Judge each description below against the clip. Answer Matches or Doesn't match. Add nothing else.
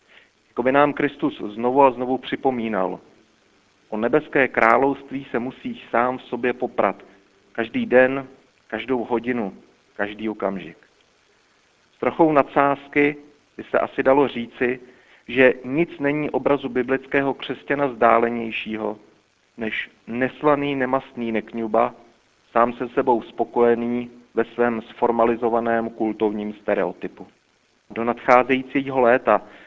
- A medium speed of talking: Doesn't match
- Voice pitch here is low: Matches